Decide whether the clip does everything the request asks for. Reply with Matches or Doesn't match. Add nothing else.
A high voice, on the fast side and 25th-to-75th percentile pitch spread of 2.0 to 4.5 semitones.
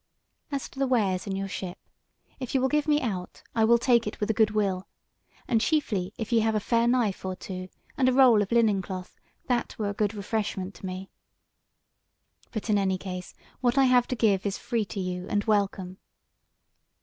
Matches